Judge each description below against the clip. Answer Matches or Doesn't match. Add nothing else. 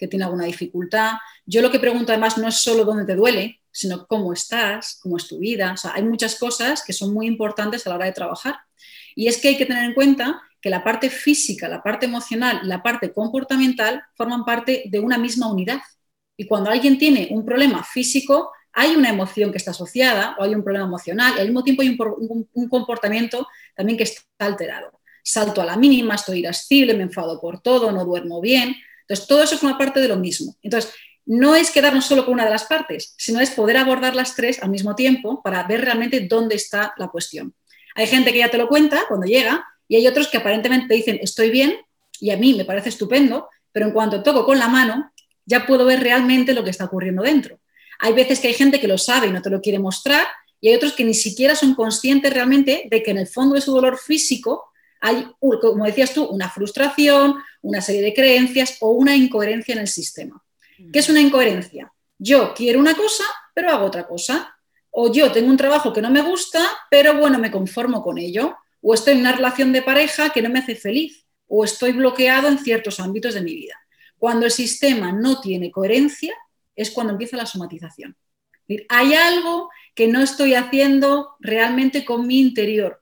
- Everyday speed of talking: Doesn't match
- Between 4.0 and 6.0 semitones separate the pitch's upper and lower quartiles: Matches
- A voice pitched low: Doesn't match